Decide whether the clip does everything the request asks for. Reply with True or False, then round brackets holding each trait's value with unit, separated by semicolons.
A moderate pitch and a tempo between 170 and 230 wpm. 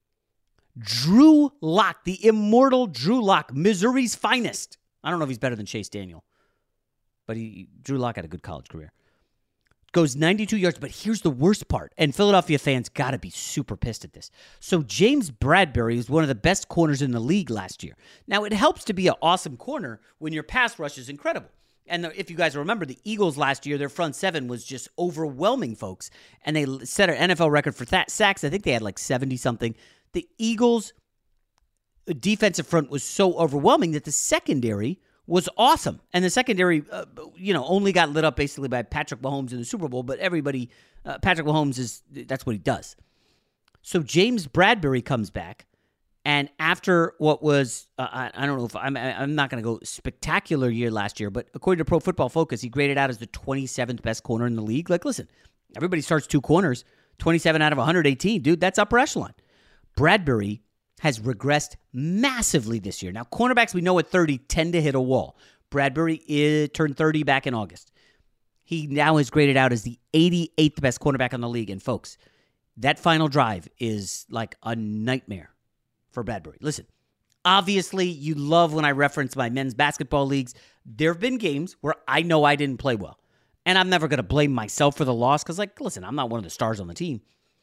True (145 Hz; 200 wpm)